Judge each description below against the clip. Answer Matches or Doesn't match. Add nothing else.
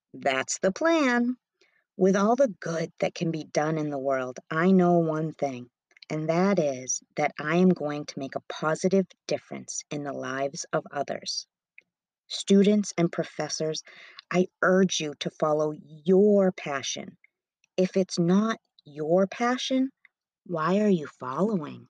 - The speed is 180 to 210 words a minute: Doesn't match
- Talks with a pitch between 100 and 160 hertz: Doesn't match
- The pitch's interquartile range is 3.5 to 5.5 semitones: Matches